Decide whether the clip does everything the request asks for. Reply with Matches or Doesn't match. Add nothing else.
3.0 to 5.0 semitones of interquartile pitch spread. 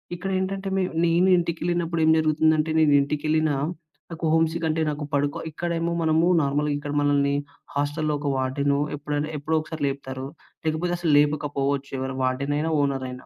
Doesn't match